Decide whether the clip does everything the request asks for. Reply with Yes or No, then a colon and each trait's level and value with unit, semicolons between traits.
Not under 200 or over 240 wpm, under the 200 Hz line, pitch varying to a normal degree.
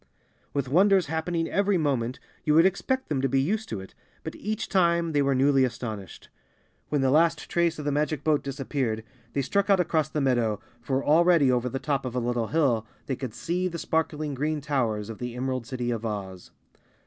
Yes: fast, 205 wpm; medium, 140 Hz; average, 4.8 semitones